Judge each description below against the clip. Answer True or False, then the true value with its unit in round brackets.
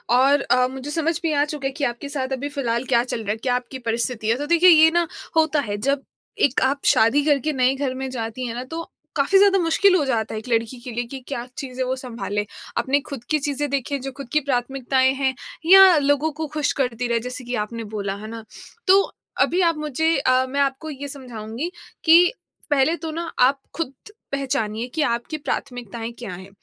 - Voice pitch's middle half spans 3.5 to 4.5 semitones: True (3.8 semitones)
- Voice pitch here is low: False (265 Hz)